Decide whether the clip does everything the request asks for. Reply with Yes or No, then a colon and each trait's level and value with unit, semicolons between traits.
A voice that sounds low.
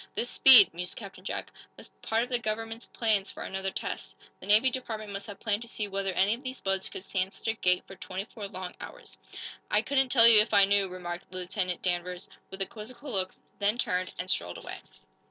No: high, 200 Hz